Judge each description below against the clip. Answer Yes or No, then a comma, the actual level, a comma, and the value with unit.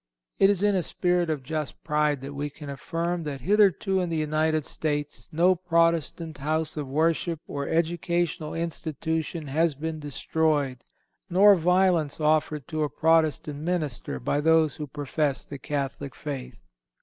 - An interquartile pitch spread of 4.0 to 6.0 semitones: No, narrow, 2.5 semitones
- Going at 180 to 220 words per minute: No, average, 150 wpm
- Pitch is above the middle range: No, medium, 155 Hz